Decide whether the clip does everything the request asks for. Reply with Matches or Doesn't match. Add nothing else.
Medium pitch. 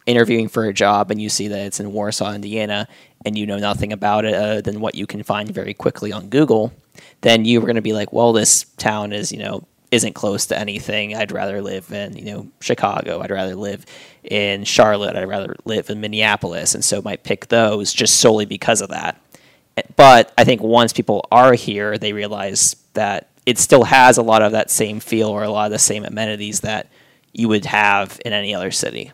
Doesn't match